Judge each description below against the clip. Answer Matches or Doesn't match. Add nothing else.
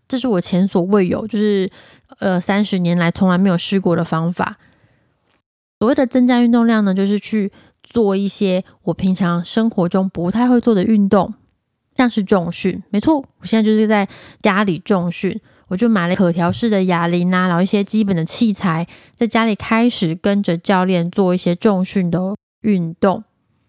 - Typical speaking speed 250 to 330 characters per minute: Matches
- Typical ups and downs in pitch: Matches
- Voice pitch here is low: Doesn't match